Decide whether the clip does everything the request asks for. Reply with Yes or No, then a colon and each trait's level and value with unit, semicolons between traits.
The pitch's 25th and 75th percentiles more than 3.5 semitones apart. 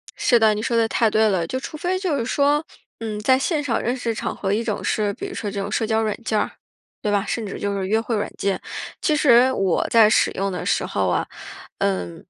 Yes: average, 4.0 semitones